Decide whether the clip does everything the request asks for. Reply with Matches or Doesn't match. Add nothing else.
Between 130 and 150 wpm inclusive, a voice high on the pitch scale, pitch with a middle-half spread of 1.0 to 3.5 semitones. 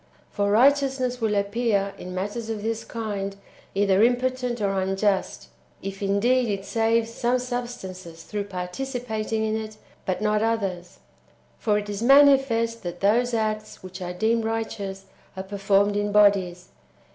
Matches